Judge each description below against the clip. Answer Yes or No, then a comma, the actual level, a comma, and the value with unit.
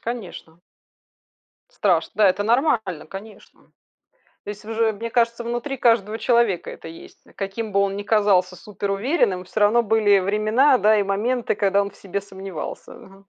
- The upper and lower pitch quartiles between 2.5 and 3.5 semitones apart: Yes, average, 2.9 semitones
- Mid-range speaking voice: No, high, 210 Hz